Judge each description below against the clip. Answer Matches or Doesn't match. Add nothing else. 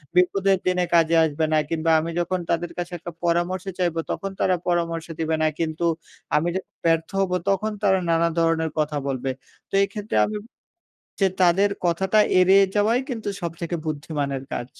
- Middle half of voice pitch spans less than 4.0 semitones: Matches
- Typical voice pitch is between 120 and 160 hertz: Doesn't match